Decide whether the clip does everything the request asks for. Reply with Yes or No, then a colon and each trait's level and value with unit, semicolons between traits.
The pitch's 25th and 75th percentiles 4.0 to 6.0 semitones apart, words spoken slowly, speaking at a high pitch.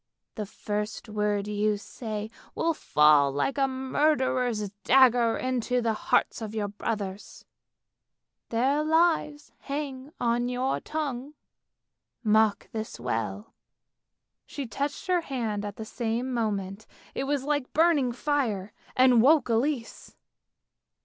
Yes: average, 4.5 semitones; slow, 125 wpm; high, 240 Hz